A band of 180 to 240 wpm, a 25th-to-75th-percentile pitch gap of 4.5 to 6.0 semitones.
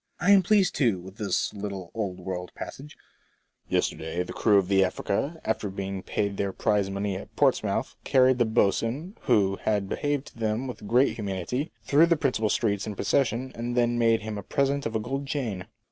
Yes: average, 195 wpm; average, 5.1 semitones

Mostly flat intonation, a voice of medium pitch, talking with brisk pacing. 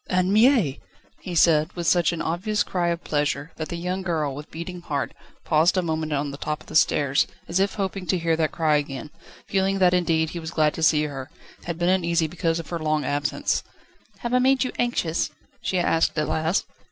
No: average, 3.0 semitones; medium, 165 Hz; fast, 215 wpm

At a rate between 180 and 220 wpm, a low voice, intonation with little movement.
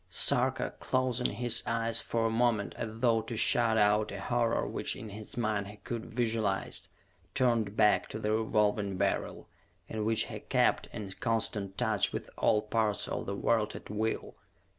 No: average, 170 wpm; low, 110 Hz; narrow, 1.7 semitones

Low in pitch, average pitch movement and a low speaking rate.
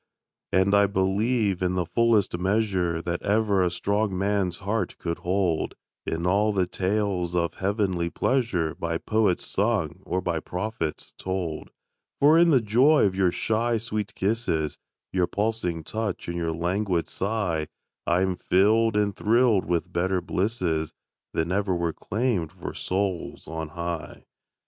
No: very low, 95 Hz; average, 3.7 semitones; average, 150 wpm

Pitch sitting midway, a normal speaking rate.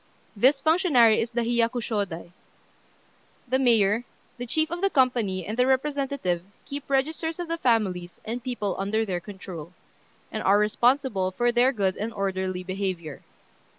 No: high, 230 Hz; average, 150 wpm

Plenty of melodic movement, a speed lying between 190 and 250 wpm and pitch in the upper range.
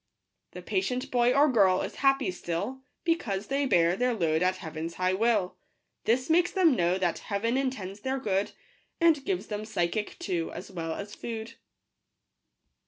No: wide, 6.2 semitones; average, 165 wpm; high, 215 Hz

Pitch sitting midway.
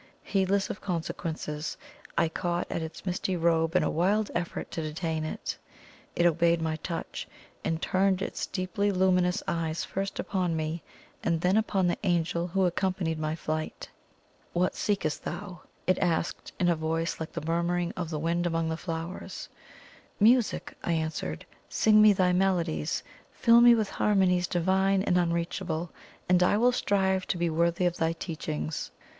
Yes: medium, 175 Hz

